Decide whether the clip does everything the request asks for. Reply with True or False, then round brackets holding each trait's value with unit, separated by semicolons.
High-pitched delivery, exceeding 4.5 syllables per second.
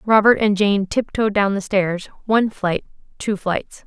False (205 Hz; 4.3 syllables/s)